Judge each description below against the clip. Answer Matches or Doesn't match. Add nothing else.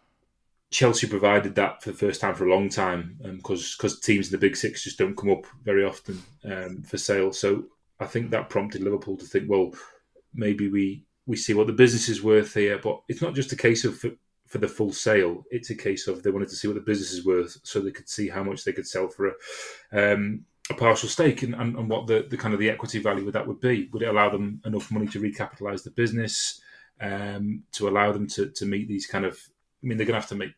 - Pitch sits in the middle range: Doesn't match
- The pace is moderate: Doesn't match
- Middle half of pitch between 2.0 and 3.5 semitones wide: Matches